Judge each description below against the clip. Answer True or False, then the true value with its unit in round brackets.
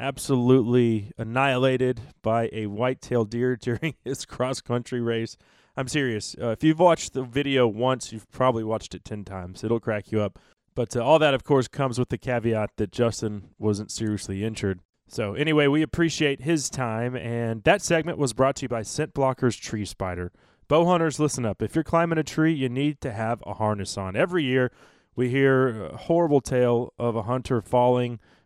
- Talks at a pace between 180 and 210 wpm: True (190 wpm)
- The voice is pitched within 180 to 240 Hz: False (125 Hz)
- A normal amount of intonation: True (3.5 semitones)